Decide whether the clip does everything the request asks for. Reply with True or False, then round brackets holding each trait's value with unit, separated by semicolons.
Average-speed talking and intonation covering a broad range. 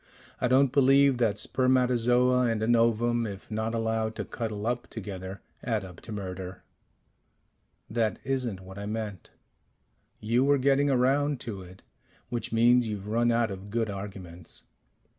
False (155 wpm; 3.4 semitones)